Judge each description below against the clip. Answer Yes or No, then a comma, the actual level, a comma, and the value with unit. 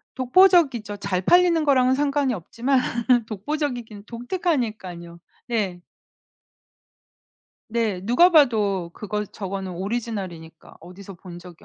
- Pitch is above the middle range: Yes, high, 220 Hz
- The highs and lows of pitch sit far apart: Yes, wide, 6.0 semitones